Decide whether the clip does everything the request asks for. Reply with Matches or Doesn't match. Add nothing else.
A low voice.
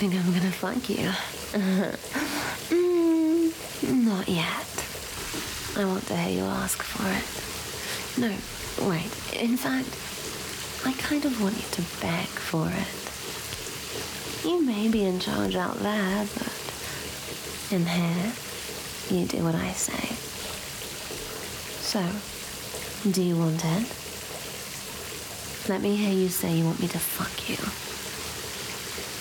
Doesn't match